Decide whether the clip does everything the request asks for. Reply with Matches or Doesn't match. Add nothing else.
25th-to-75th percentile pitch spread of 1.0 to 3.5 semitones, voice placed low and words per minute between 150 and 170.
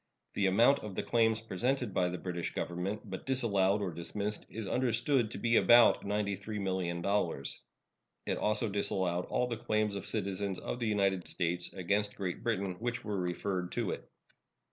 Matches